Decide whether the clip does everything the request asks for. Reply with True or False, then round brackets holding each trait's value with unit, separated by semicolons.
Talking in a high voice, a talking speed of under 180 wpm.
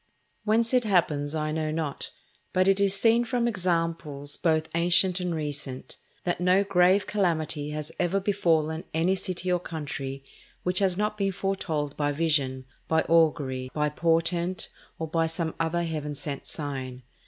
False (165 Hz; 155 wpm)